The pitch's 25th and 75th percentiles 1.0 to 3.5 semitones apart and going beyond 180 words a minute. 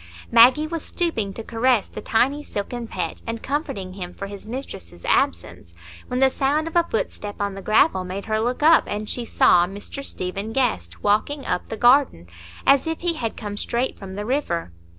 No: wide, 5.5 semitones; average, 190 wpm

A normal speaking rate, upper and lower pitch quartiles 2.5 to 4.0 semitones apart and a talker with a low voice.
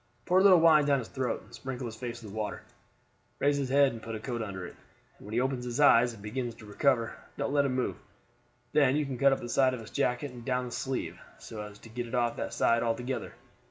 No: fast, 260 wpm; average, 2.9 semitones; low, 125 Hz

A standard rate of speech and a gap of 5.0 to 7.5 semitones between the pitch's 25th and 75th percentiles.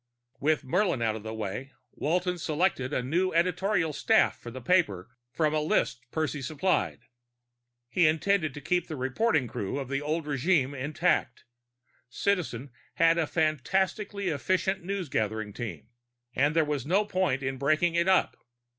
Yes: average, 155 wpm; wide, 5.6 semitones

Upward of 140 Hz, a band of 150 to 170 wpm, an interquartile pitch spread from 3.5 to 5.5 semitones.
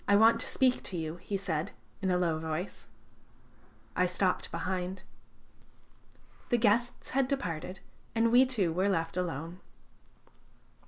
No: medium, 185 Hz; average, 140 wpm; average, 4.9 semitones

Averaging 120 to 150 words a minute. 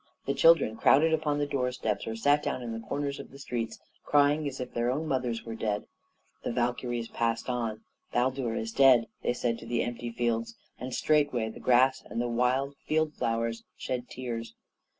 No: average, 190 wpm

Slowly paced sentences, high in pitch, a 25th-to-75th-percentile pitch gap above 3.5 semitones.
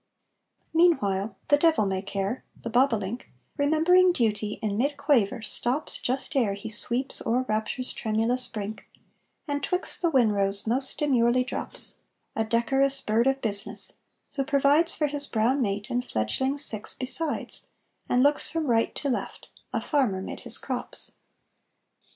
No: average, 145 wpm; very high, 250 Hz; average, 4.8 semitones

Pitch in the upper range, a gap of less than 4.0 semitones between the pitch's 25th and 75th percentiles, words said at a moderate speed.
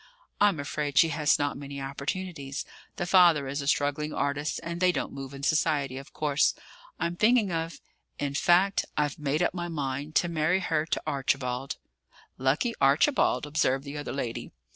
No: medium, 150 Hz; average, 3.4 semitones; average, 170 wpm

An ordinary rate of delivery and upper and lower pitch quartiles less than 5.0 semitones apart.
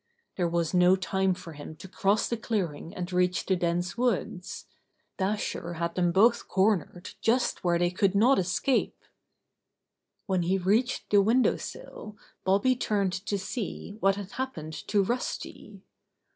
Yes: average, 150 wpm; average, 3.1 semitones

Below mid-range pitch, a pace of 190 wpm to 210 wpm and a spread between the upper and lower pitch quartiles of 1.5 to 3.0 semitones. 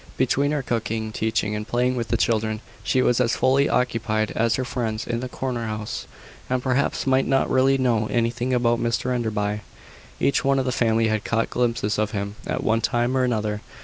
Yes: low, 120 Hz; average, 200 wpm; average, 2.7 semitones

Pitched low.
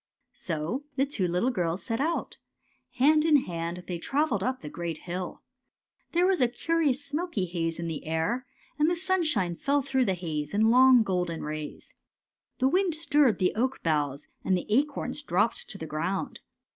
No: high, 225 Hz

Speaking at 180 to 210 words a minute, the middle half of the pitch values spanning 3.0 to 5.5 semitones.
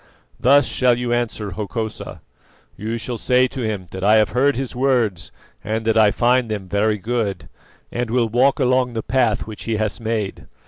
No: average, 185 wpm; narrow, 2.6 semitones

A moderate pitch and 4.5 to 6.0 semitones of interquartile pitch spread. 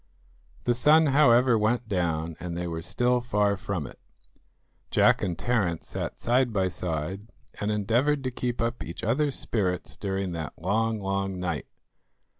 No: low, 105 Hz; average, 5.2 semitones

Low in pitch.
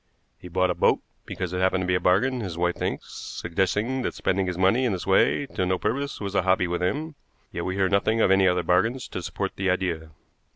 Yes: very low, 95 Hz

